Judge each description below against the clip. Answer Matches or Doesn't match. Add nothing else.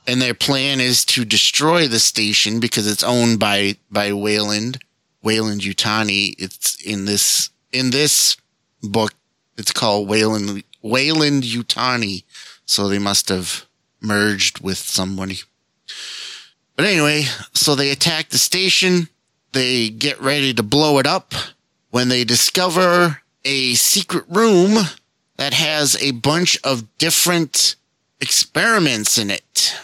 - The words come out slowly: Matches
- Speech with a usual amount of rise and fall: Doesn't match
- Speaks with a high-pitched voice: Doesn't match